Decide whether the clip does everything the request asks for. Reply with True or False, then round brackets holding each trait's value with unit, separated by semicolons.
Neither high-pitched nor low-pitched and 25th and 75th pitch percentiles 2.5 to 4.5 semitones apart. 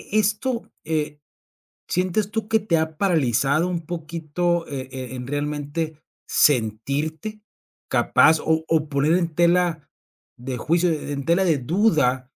True (160 Hz; 3.6 semitones)